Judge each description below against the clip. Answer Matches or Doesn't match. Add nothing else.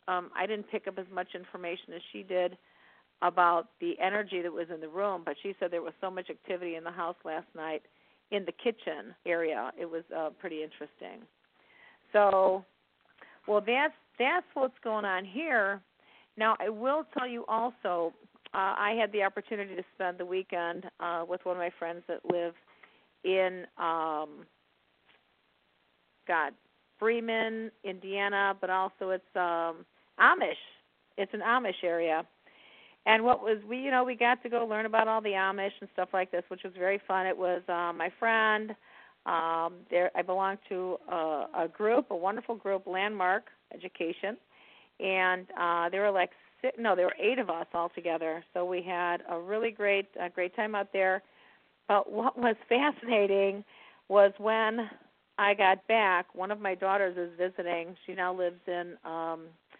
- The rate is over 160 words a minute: Matches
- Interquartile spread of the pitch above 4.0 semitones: Doesn't match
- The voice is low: Doesn't match